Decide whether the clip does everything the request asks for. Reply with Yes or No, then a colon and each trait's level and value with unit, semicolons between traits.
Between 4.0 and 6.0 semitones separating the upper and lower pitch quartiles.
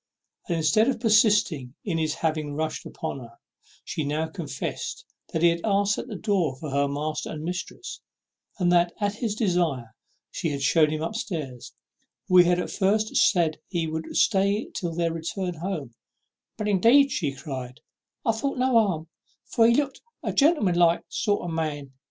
Yes: average, 5.0 semitones